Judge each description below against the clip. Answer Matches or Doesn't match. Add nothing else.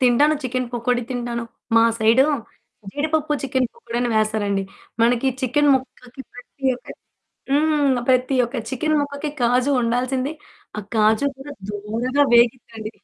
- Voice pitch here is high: Matches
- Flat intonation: Doesn't match